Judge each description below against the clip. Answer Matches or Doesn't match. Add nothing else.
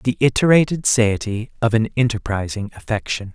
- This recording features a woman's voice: Doesn't match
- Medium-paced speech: Doesn't match